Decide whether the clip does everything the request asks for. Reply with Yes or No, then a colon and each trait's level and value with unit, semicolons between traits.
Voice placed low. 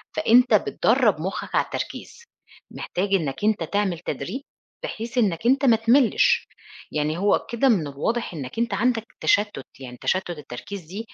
No: high, 205 Hz